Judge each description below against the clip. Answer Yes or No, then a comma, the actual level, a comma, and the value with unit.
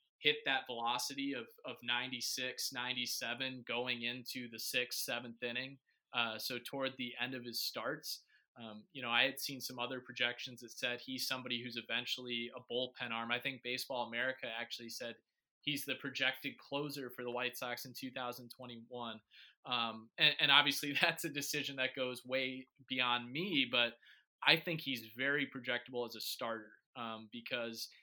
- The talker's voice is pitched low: Yes, low, 125 Hz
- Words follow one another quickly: No, average, 165 wpm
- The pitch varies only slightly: Yes, narrow, 1.7 semitones